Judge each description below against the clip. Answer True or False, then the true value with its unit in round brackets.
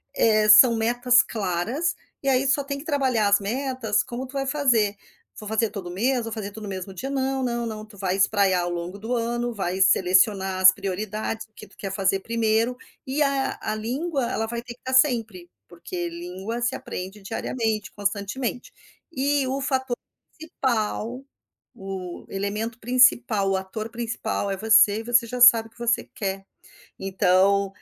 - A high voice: True (220 Hz)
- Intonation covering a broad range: False (4.1 semitones)